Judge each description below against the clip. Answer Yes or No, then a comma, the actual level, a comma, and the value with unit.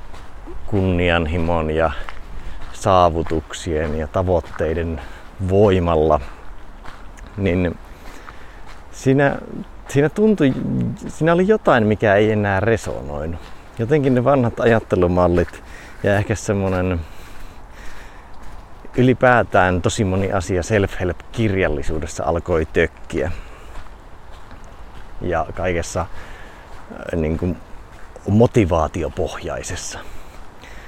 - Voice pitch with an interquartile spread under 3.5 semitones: No, average, 4.8 semitones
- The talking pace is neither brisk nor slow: No, slow, 75 wpm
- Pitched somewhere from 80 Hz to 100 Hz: Yes, very low, 90 Hz